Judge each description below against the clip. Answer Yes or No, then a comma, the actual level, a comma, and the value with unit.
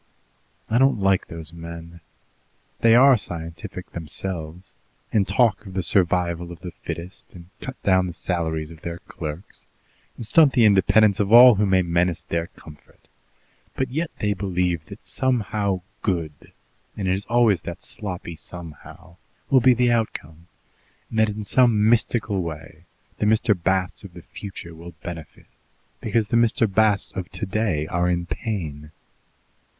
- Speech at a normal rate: Yes, average, 155 wpm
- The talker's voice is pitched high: No, very low, 95 Hz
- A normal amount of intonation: Yes, average, 4.4 semitones